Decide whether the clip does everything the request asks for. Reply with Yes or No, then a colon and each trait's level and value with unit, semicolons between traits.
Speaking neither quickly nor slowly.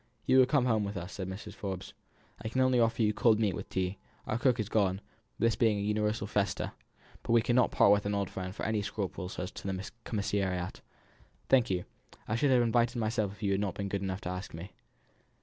No: fast, 235 wpm